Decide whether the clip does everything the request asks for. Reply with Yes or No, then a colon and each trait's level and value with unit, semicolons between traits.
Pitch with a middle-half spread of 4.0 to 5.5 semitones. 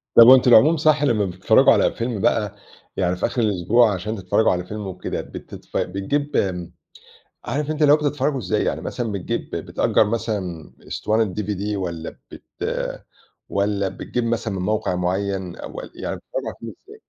Yes: average, 4.6 semitones